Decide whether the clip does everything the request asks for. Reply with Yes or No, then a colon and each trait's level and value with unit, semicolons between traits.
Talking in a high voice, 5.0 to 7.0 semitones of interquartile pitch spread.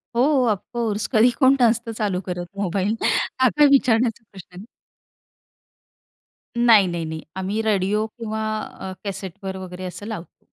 No: high, 205 Hz; average, 3.5 semitones